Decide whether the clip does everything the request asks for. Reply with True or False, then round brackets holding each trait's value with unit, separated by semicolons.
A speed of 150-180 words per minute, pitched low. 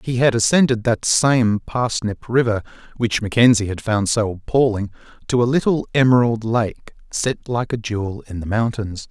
True (165 wpm; 115 Hz)